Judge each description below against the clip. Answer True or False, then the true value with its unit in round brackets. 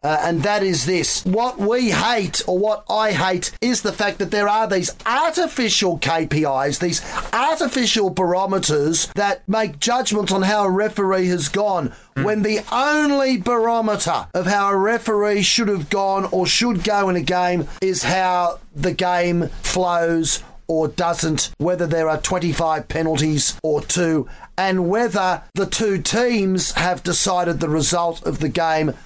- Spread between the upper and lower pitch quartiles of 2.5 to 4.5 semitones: True (3.8 semitones)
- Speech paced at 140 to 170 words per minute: True (155 wpm)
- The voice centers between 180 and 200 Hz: True (185 Hz)